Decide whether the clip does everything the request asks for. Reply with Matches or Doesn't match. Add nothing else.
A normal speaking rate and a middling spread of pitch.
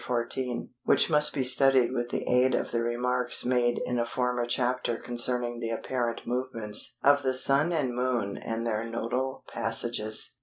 Doesn't match